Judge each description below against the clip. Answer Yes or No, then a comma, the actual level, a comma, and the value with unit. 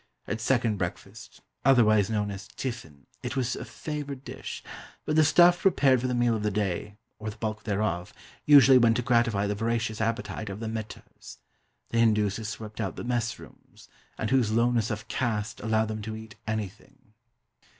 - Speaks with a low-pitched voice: Yes, low, 110 Hz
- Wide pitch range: No, narrow, 2.6 semitones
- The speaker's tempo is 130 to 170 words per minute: No, average, 180 wpm